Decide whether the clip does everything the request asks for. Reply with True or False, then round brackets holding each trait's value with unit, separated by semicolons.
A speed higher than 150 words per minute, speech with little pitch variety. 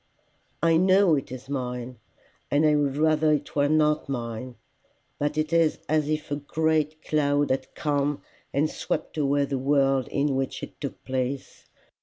True (165 wpm; 2.3 semitones)